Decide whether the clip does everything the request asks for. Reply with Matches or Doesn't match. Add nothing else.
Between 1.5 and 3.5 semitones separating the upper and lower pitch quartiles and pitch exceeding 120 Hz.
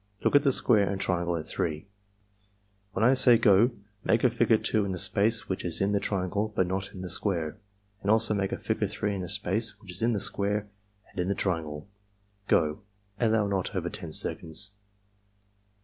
Doesn't match